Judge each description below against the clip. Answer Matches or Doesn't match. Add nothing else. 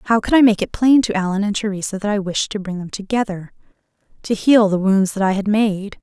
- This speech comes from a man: Doesn't match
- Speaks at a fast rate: Matches